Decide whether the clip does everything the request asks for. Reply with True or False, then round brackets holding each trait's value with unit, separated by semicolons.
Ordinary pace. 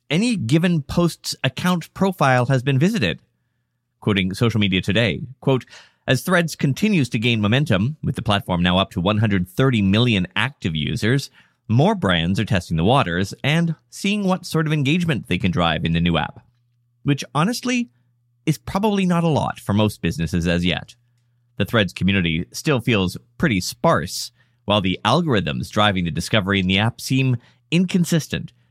True (165 wpm)